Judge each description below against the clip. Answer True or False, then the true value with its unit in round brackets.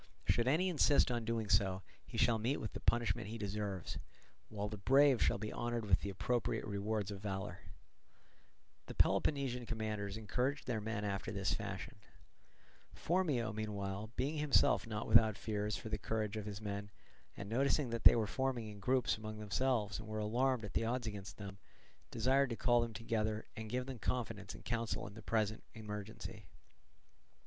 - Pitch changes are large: False (2.7 semitones)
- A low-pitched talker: True (110 Hz)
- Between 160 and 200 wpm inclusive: True (175 wpm)